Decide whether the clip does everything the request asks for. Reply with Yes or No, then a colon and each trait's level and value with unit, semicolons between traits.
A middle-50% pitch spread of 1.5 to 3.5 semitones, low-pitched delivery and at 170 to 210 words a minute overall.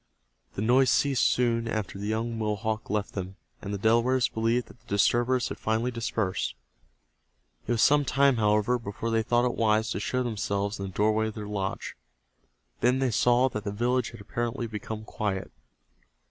Yes: narrow, 2.5 semitones; low, 110 Hz; average, 180 wpm